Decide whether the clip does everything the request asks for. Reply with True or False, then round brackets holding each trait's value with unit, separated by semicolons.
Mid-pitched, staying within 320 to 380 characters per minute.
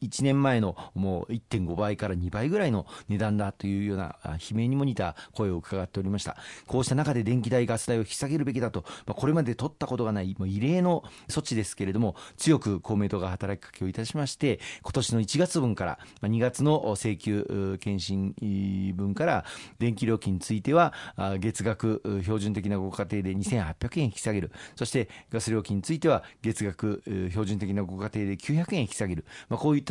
False (105 Hz; 355 characters per minute)